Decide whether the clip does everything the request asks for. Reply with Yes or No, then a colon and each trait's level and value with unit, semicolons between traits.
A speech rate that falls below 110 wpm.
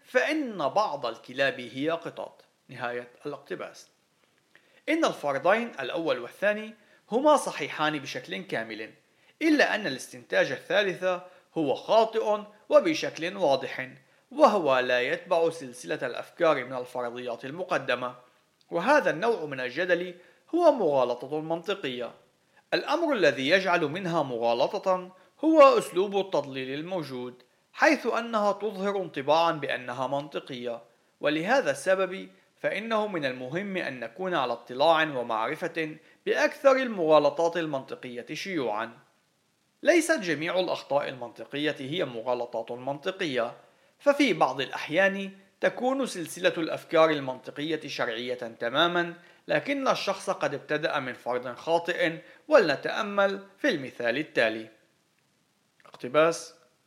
Yes: average, 100 wpm